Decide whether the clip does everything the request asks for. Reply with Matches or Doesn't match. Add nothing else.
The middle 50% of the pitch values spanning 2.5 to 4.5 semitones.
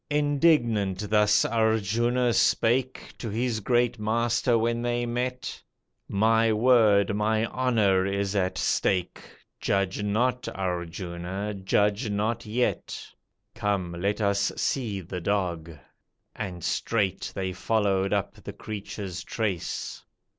Matches